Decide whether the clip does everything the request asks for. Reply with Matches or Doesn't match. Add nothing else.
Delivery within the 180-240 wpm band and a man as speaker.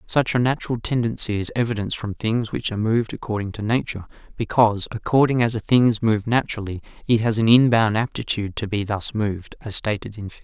Matches